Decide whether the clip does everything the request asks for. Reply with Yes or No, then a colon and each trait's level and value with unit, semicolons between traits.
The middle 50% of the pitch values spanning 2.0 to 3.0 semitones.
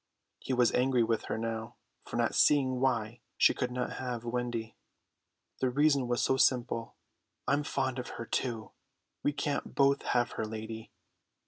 Yes: narrow, 2.4 semitones